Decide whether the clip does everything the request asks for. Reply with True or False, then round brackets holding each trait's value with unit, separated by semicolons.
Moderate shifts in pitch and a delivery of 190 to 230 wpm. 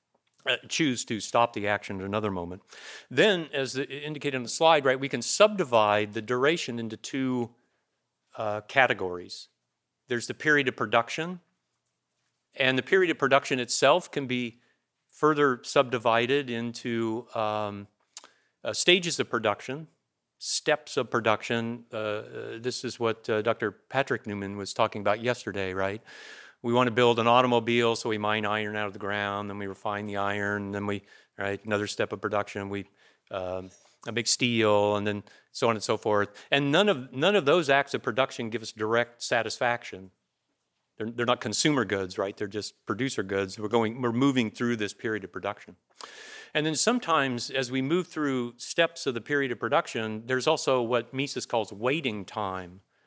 False (4.1 semitones; 175 wpm)